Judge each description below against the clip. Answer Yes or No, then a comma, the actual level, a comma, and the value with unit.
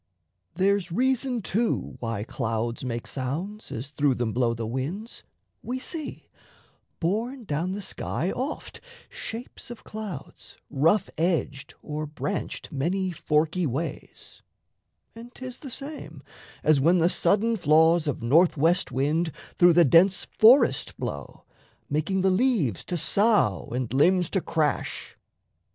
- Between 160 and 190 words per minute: No, slow, 135 wpm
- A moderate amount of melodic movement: No, wide, 6.9 semitones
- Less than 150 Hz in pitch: No, medium, 170 Hz